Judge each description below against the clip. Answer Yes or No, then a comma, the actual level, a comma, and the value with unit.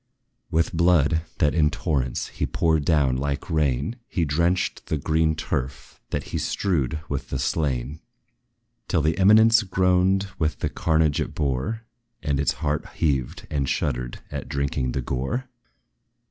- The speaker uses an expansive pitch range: No, average, 3.9 semitones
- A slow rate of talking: No, average, 145 wpm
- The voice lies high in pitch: No, very low, 75 Hz